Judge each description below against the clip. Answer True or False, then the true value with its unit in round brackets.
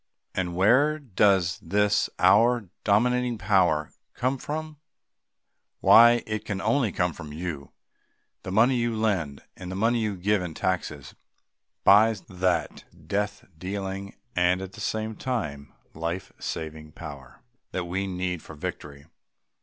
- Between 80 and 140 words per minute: True (135 wpm)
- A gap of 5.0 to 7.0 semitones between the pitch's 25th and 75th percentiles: False (4.2 semitones)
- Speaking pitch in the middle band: False (95 Hz)